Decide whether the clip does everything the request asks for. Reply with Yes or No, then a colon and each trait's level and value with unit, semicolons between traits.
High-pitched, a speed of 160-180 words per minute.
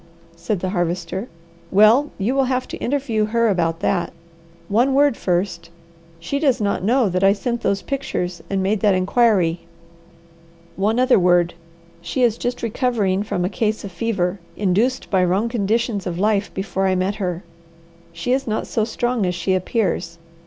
Yes: high, 200 Hz; average, 170 wpm